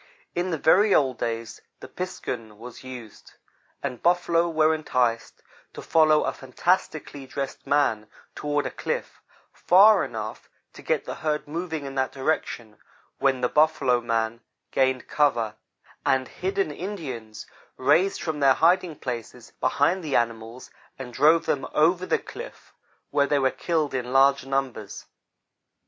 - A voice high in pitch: No, medium, 140 Hz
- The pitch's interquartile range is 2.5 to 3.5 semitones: No, average, 4.6 semitones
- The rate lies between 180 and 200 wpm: No, average, 145 wpm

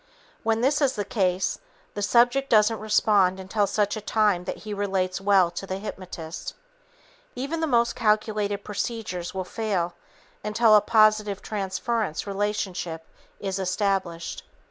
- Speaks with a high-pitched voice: Yes, high, 205 Hz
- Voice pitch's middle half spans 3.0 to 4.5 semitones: No, narrow, 2.6 semitones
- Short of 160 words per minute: Yes, slow, 135 wpm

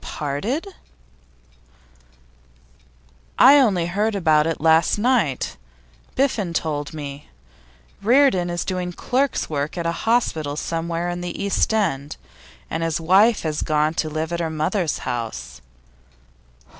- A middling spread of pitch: Yes, average, 4.8 semitones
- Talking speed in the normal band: No, slow, 125 wpm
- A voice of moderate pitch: Yes, medium, 170 Hz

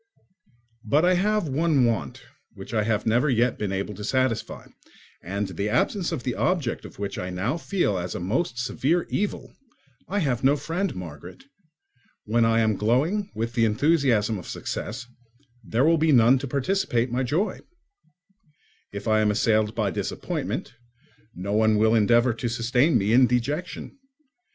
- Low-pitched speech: Yes, low, 120 Hz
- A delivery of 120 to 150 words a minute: No, average, 165 wpm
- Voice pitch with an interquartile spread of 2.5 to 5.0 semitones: No, wide, 5.6 semitones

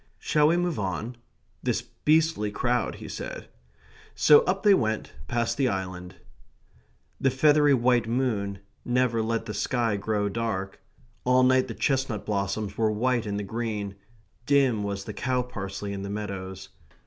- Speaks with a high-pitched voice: No, low, 115 Hz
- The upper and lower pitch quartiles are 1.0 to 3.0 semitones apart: No, average, 4.2 semitones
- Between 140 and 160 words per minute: Yes, average, 155 wpm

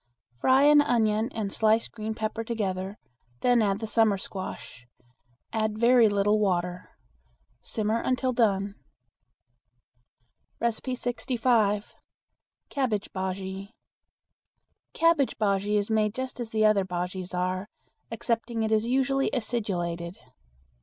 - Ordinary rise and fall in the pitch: Yes, average, 3.1 semitones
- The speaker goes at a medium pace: No, slow, 105 wpm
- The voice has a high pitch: Yes, high, 215 Hz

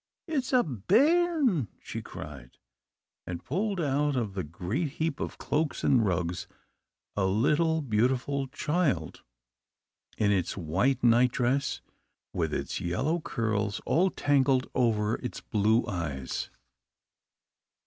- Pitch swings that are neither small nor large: No, wide, 7.3 semitones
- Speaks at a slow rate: Yes, slow, 115 wpm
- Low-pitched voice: Yes, low, 125 Hz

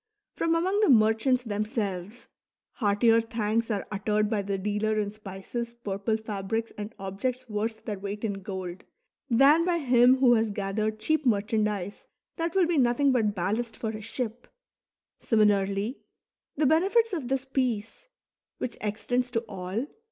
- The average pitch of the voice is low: No, high, 220 Hz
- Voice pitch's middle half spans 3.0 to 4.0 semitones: Yes, average, 3.5 semitones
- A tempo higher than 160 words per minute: No, average, 150 wpm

